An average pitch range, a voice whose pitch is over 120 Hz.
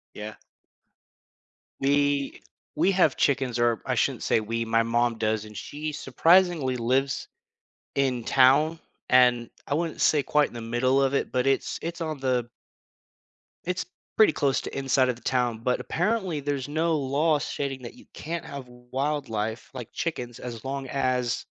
Yes: average, 3.5 semitones; low, 135 Hz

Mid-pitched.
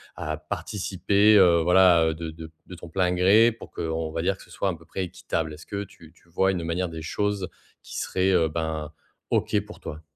No: very low, 85 Hz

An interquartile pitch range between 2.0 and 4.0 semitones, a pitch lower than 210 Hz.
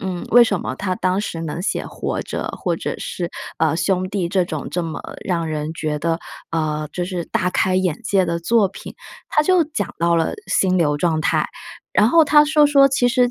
No: average, 5.2 semitones; medium, 185 Hz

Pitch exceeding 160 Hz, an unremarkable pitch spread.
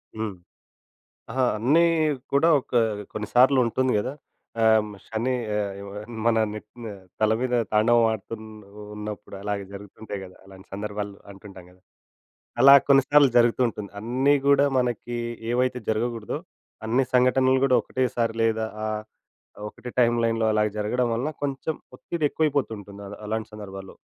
No: low, 115 Hz; average, 3.3 semitones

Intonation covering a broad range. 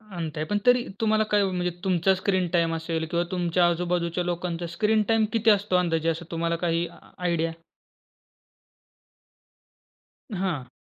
No: narrow, 2.4 semitones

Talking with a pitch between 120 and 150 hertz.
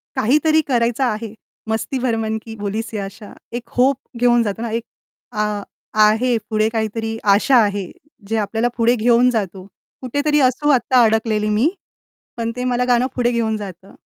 No: high, 230 Hz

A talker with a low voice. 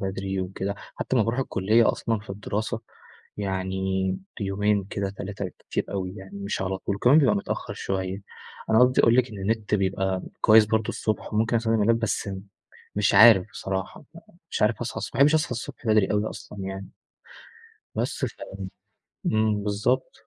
Yes: low, 105 Hz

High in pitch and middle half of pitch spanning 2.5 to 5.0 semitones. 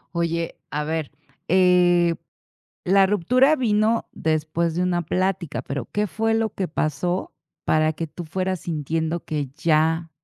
No: medium, 170 Hz; average, 3.1 semitones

